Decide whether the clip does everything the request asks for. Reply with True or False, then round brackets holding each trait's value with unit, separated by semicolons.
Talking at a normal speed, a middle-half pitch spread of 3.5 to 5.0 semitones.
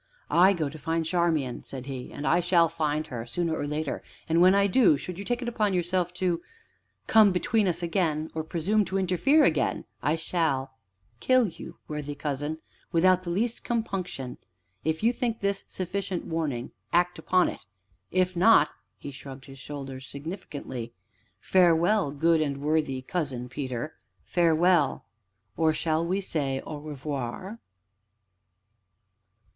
True (150 wpm; 4.2 semitones)